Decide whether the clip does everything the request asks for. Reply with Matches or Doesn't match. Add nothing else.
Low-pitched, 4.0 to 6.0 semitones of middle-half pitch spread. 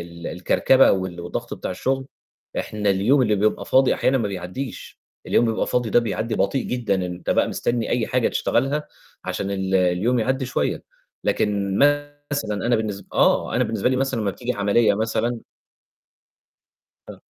Matches